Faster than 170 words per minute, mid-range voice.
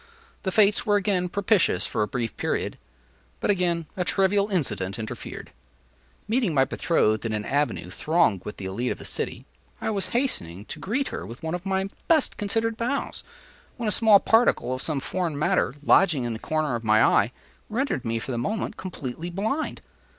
Yes: average, 185 wpm; medium, 175 Hz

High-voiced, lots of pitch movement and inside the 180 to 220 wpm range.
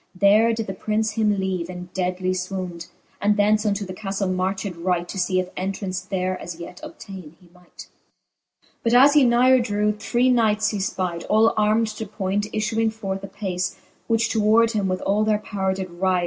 No: high, 200 Hz; average, 2.7 semitones; average, 190 wpm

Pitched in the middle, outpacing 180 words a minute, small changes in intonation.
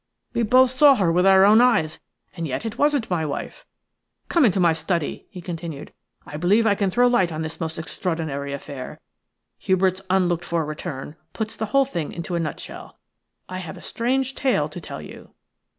No: medium, 180 Hz; average, 190 wpm; wide, 5.6 semitones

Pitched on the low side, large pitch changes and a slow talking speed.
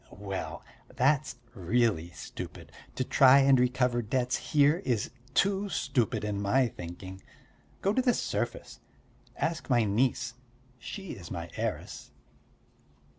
Yes: low, 125 Hz; wide, 5.7 semitones; slow, 125 wpm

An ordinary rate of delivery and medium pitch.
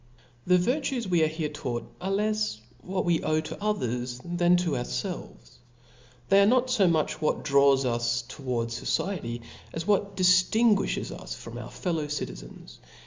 Yes: average, 155 wpm; medium, 165 Hz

